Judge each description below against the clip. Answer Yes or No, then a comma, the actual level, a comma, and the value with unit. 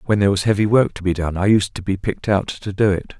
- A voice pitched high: No, low, 100 Hz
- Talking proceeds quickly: Yes, fast, 320 wpm